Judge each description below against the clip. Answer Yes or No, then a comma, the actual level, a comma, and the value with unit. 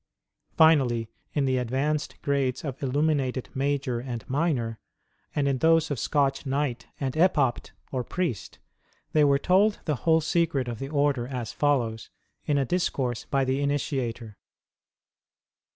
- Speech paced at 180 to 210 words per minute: No, average, 140 wpm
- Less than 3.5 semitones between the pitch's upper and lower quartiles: Yes, average, 2.9 semitones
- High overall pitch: No, medium, 140 Hz